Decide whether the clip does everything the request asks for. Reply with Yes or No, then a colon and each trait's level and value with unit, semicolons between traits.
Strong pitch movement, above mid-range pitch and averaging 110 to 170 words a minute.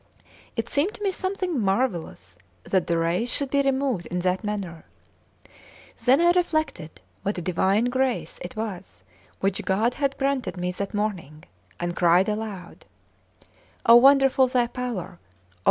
Yes: wide, 6.8 semitones; high, 220 Hz; average, 140 wpm